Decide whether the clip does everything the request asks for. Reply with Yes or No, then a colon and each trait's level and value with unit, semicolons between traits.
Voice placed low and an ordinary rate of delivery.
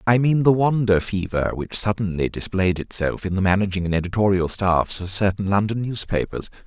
Yes: low, 100 Hz; average, 170 wpm